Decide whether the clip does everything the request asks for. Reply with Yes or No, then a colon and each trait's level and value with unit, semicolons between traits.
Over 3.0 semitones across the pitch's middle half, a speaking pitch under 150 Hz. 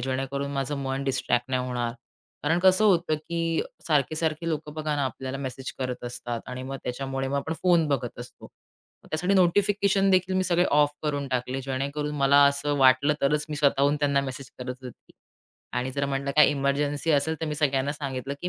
No: average, 2.7 semitones; medium, 140 Hz